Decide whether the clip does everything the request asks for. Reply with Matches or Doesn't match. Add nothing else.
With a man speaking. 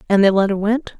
Doesn't match